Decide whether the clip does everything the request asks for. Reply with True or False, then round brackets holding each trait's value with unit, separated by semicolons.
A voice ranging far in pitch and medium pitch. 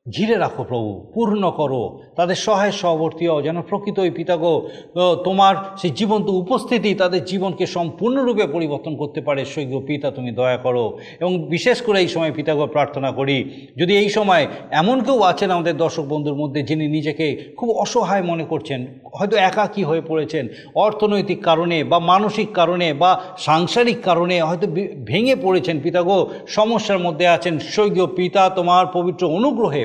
False (4.0 semitones; 175 Hz)